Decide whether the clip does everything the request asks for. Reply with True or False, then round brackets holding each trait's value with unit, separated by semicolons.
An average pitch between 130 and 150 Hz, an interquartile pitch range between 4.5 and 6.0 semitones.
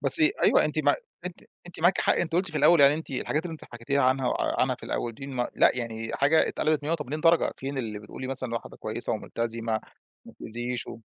True (135 Hz; 5.1 semitones)